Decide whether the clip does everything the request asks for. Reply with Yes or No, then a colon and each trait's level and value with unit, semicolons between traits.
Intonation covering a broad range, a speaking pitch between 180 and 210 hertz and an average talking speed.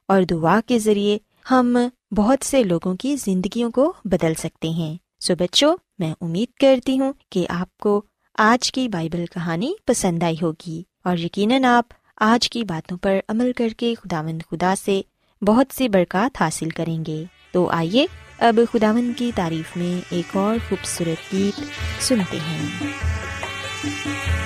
Yes: wide, 6.0 semitones; high, 190 Hz; average, 150 wpm